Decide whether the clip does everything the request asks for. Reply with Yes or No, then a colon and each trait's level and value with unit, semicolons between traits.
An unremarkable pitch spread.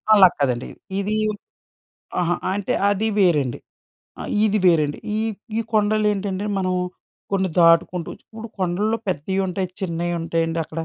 Yes: average, 3.4 semitones